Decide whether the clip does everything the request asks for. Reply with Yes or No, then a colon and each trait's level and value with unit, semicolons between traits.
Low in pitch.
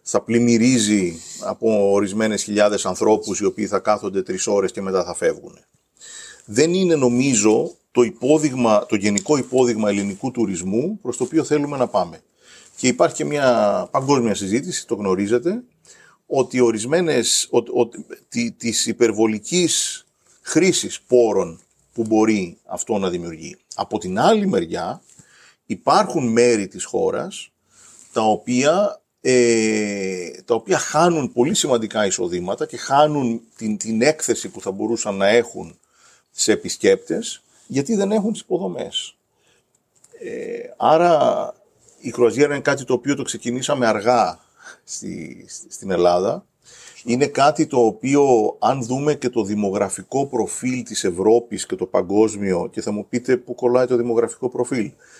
Yes: low, 120 Hz